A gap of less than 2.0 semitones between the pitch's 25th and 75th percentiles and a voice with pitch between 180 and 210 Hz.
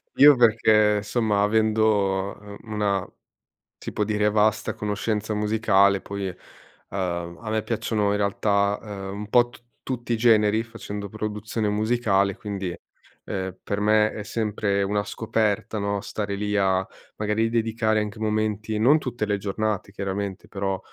No: narrow, 1.4 semitones; low, 105 Hz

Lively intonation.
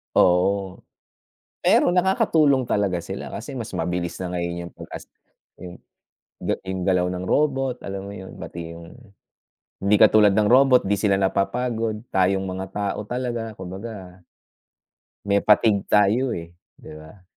No: average, 3.7 semitones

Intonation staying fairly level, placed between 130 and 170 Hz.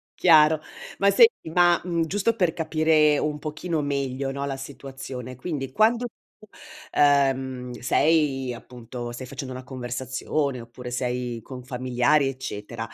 No: average, 3.8 semitones; low, 135 Hz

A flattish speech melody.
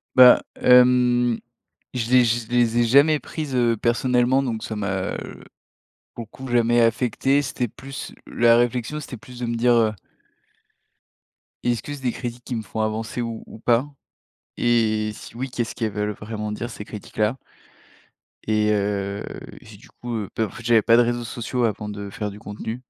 Yes: narrow, 2.2 semitones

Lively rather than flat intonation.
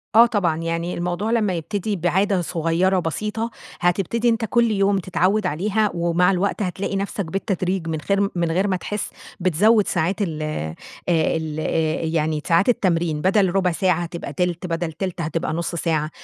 No: average, 3.2 semitones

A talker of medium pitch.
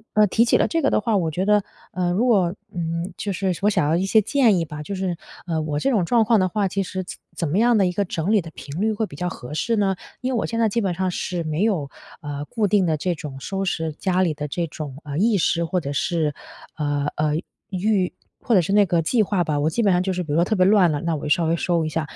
Yes: medium, 180 Hz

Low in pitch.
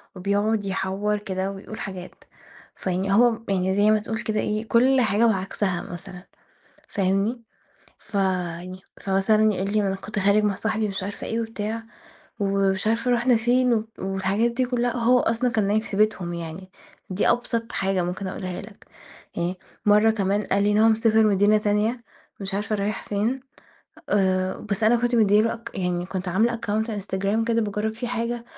No: high, 210 Hz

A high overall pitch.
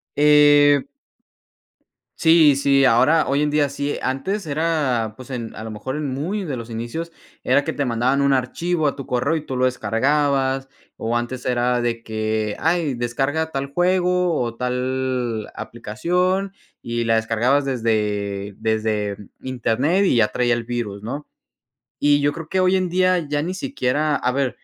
No: low, 135 Hz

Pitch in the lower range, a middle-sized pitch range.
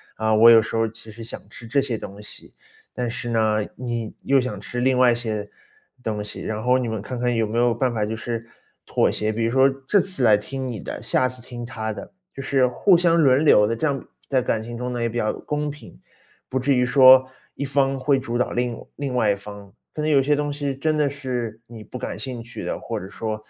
Yes: low, 120 Hz; average, 3.0 semitones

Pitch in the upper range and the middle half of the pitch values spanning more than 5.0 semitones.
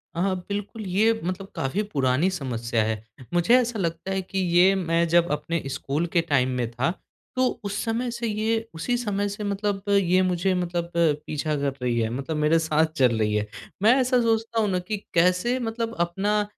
No: medium, 180 Hz; wide, 5.5 semitones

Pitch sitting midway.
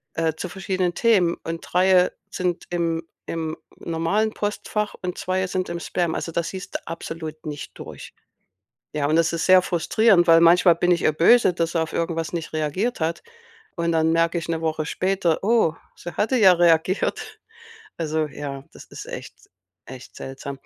Yes: medium, 170 Hz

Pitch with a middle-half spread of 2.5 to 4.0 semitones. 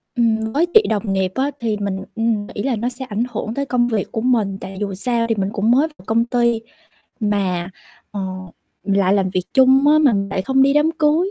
No: average, 4.7 semitones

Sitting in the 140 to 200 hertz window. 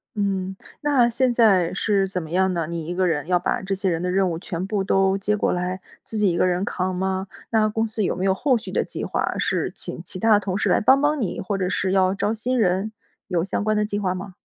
Yes: high, 195 Hz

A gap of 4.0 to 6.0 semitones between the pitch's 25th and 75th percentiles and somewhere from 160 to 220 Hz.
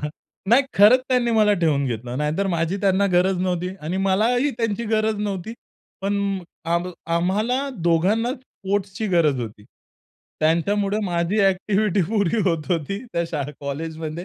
Yes: average, 4.3 semitones; high, 190 Hz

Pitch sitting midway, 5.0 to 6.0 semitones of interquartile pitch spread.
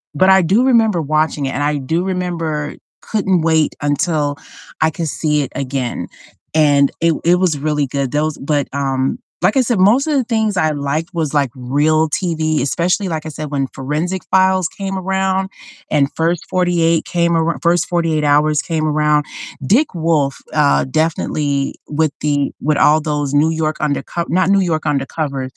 No: medium, 155 Hz; average, 3.3 semitones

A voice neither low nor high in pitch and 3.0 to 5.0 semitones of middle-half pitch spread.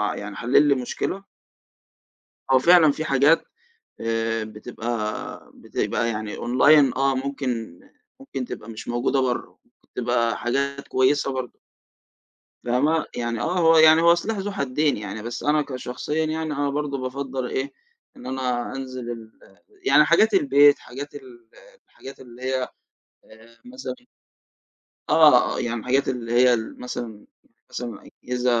No: low, 130 Hz; average, 3.3 semitones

